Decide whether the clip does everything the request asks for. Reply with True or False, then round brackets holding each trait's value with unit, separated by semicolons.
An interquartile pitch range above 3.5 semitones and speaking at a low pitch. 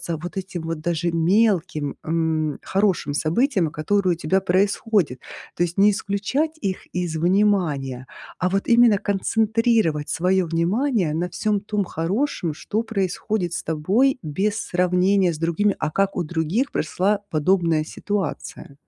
False (4.0 semitones; 185 Hz)